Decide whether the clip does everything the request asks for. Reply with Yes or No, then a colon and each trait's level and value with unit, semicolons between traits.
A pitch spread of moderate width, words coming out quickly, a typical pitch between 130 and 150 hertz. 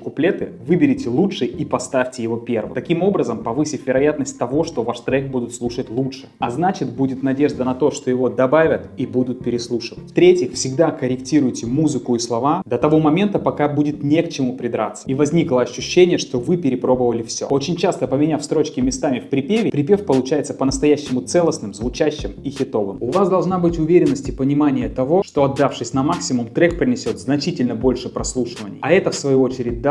Yes: average, 3.7 semitones; fast, 180 wpm; low, 135 Hz